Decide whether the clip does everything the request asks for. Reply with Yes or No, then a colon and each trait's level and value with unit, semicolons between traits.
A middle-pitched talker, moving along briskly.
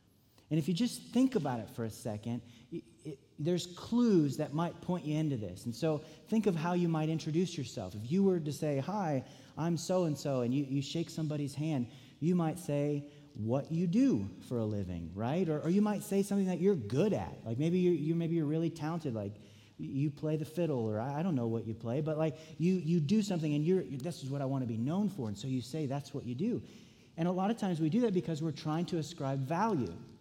Yes: medium, 155 Hz; fast, 250 wpm